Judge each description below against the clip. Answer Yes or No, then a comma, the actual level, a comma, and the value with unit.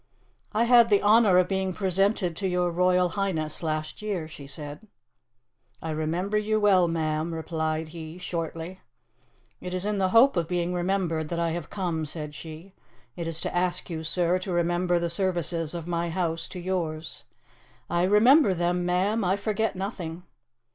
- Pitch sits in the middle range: Yes, medium, 175 Hz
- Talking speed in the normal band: Yes, average, 170 wpm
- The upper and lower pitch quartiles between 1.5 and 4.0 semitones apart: Yes, average, 2.7 semitones